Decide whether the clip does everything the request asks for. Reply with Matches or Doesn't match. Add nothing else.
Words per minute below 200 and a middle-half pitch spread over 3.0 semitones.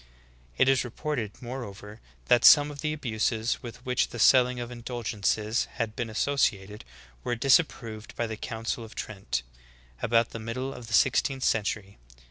Doesn't match